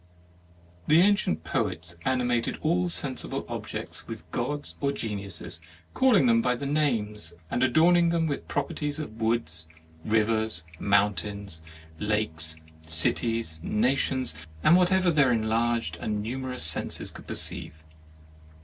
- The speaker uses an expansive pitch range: Yes, wide, 6.1 semitones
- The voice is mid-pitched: No, low, 115 Hz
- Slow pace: Yes, slow, 130 wpm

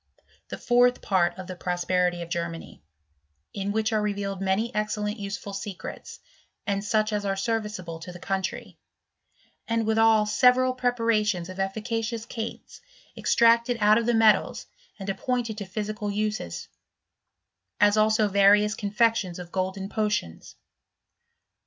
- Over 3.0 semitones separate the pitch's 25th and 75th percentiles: No, narrow, 2.5 semitones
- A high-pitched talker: Yes, high, 210 Hz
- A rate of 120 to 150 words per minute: Yes, slow, 135 wpm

